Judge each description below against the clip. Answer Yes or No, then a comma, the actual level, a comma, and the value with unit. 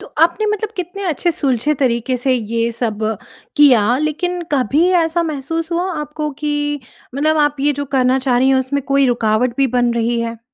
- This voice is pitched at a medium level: No, very high, 275 Hz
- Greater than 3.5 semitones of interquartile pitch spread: Yes, average, 4.0 semitones